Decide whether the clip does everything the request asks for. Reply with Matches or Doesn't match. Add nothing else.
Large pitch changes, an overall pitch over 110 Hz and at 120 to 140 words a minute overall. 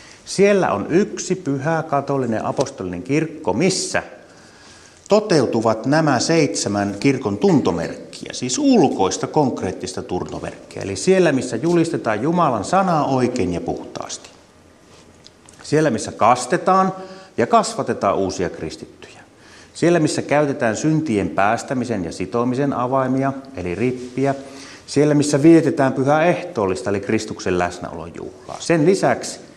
Doesn't match